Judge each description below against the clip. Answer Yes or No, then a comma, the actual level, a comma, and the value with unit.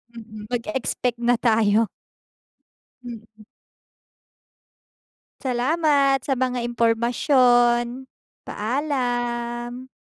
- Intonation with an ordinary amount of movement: No, narrow, 1.6 semitones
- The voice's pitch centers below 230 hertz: No, high, 240 Hz